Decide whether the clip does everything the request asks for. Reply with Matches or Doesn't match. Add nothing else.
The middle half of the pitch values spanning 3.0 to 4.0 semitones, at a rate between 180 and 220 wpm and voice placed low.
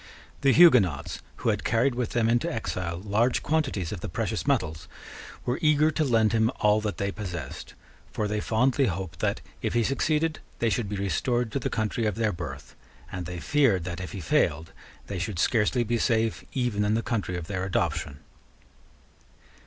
Doesn't match